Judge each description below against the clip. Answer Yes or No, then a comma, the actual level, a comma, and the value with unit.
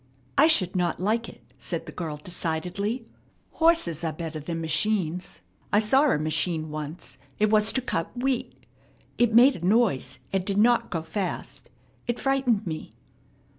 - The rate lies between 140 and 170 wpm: Yes, average, 160 wpm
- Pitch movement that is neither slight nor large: No, wide, 6.3 semitones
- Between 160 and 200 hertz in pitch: Yes, medium, 185 Hz